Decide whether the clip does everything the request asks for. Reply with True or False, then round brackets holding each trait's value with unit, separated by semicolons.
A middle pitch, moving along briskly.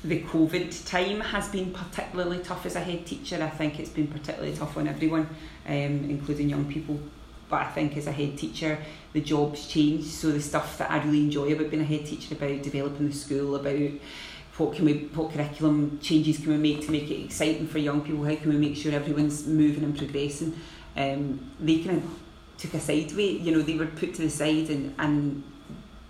True (150 Hz; 215 wpm)